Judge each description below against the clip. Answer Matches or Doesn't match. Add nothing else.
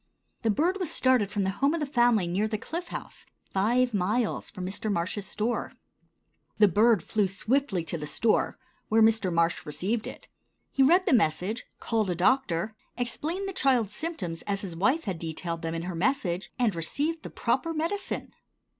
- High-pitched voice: Matches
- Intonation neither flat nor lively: Doesn't match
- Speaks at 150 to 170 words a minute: Doesn't match